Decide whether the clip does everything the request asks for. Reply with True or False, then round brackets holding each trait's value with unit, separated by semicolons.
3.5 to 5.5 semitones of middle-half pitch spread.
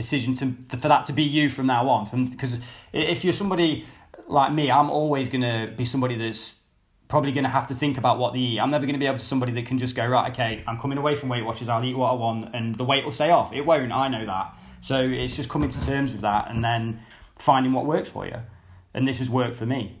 False (3.0 semitones)